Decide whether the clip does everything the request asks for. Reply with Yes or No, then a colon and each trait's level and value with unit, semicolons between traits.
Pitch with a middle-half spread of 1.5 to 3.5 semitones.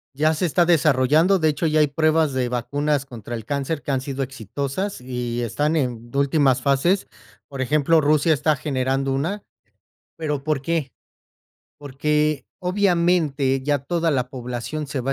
Yes: average, 3.1 semitones